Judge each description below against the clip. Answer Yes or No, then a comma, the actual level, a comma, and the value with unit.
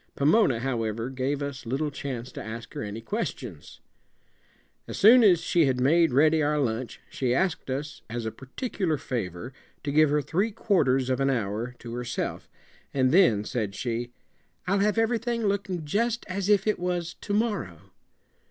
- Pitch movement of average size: No, wide, 7.6 semitones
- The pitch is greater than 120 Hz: Yes, medium, 140 Hz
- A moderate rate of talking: Yes, average, 170 wpm